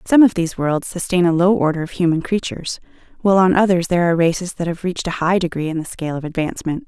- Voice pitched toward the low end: No, medium, 175 Hz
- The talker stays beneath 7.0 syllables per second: No, 7.1 syllables/s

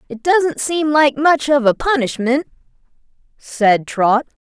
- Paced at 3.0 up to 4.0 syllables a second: Yes, 3.8 syllables/s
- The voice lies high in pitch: Yes, very high, 275 Hz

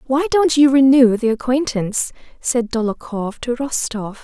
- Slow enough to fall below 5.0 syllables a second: Yes, 4.6 syllables/s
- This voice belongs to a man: No, female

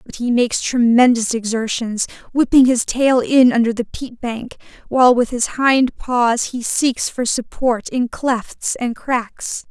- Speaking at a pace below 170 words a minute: Yes, average, 160 wpm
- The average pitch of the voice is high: Yes, high, 240 Hz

